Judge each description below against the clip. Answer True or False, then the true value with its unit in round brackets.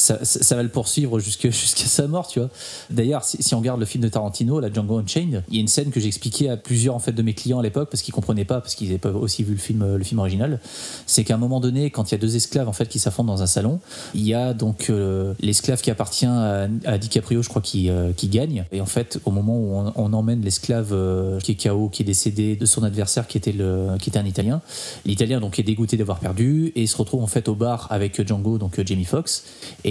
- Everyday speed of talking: False (275 wpm)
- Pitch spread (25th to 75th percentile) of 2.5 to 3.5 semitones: True (3.1 semitones)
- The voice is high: False (115 Hz)